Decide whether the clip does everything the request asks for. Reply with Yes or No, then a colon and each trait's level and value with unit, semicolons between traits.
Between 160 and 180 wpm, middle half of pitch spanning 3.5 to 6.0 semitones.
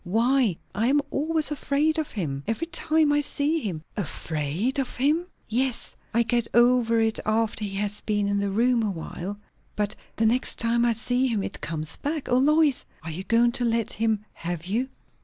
No: average, 195 wpm; average, 4.7 semitones